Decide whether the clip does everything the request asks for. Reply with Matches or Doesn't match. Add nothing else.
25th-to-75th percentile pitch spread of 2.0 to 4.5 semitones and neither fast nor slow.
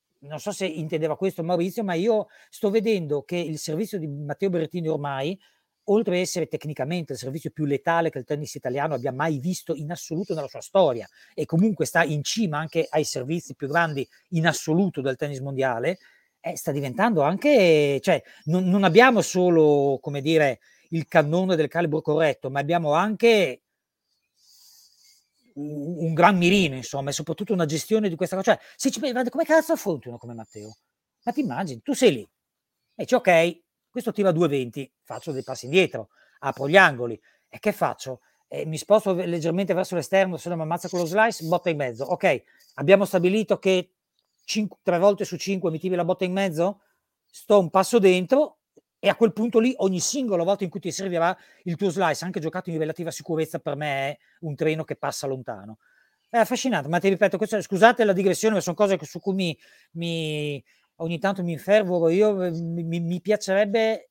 Doesn't match